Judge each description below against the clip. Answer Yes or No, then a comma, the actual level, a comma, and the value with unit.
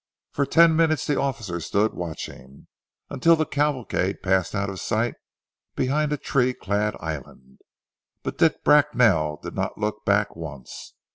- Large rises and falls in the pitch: Yes, wide, 8.5 semitones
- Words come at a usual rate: Yes, average, 145 wpm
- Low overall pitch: Yes, low, 105 Hz